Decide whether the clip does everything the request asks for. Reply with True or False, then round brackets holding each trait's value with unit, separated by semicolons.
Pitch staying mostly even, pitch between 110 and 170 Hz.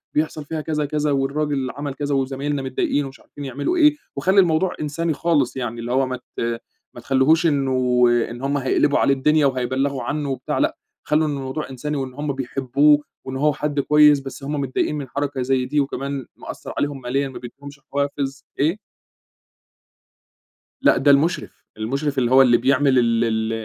True (2.1 semitones; 140 Hz)